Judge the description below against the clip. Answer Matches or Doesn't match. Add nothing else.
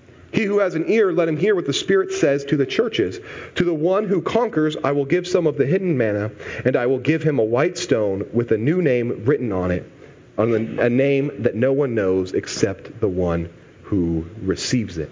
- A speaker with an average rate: Doesn't match